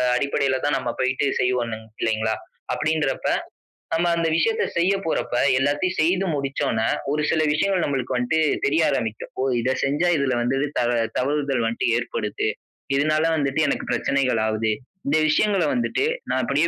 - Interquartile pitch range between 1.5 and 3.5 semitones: No, average, 4.3 semitones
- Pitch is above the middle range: No, medium, 140 Hz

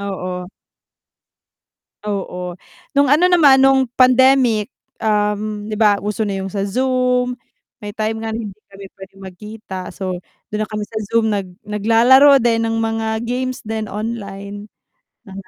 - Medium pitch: No, high, 215 Hz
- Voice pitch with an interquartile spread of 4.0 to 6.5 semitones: No, average, 3.6 semitones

